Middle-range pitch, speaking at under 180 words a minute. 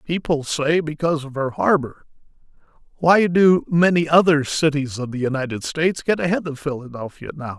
Yes: medium, 150 Hz; average, 160 wpm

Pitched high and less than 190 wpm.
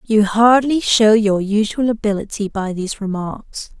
Yes: high, 215 Hz; average, 140 wpm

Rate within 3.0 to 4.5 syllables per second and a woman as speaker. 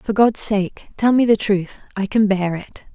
Yes: 4.4 syllables/s; female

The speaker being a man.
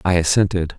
Yes: male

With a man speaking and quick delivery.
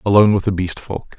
Yes: male; fast, 255 wpm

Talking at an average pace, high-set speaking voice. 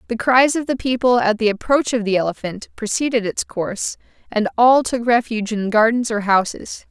Yes: average, 190 wpm; high, 230 Hz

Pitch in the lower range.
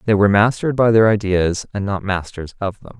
Yes: low, 100 Hz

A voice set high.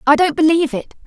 Yes: very high, 305 Hz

